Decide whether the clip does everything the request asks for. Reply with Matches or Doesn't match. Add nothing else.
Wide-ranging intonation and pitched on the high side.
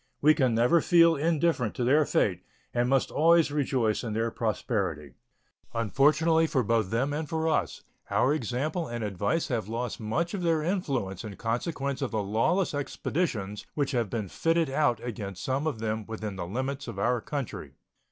Doesn't match